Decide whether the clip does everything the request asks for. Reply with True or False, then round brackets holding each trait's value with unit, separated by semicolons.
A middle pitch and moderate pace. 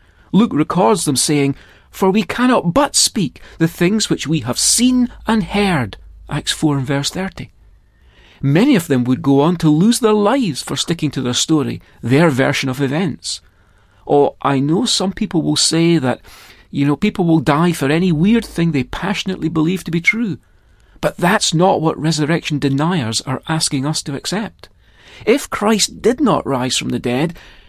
True (160 Hz; 180 wpm)